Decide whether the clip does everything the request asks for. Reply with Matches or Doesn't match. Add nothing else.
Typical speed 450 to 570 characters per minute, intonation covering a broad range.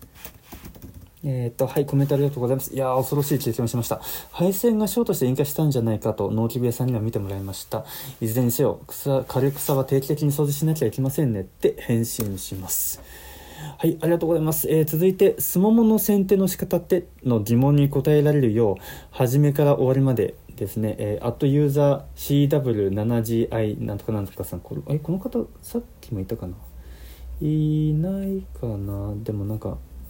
Doesn't match